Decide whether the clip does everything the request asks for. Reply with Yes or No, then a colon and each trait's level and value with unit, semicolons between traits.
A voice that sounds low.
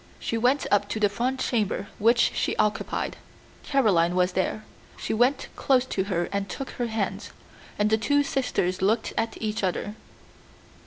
No: high, 215 Hz